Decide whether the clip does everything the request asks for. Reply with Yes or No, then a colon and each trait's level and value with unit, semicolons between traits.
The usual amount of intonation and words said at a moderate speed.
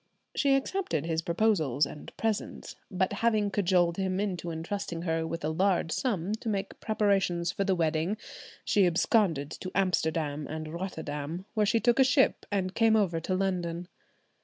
Yes: average, 3.9 semitones; average, 160 wpm